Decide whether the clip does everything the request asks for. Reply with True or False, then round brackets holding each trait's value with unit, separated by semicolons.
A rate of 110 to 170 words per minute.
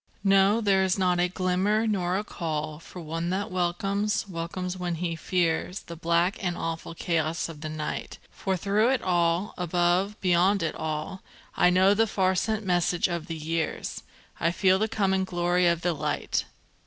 False (180 wpm)